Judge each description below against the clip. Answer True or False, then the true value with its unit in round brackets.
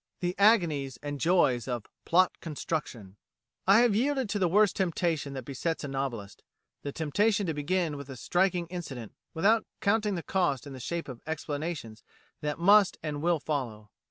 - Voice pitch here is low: False (160 Hz)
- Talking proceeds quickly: False (170 wpm)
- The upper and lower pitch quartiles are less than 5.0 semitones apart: False (5.3 semitones)